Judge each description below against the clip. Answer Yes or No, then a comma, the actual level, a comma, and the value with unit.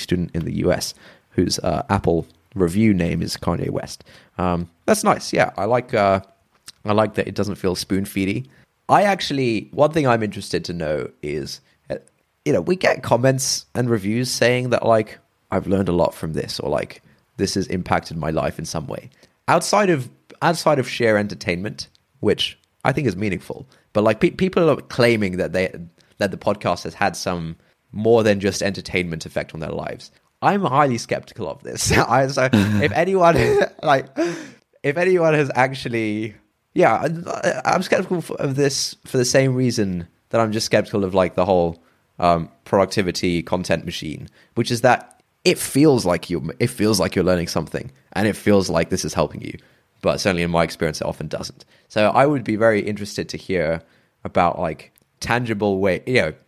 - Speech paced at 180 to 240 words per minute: Yes, average, 185 wpm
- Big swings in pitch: Yes, wide, 5.7 semitones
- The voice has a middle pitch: No, low, 105 Hz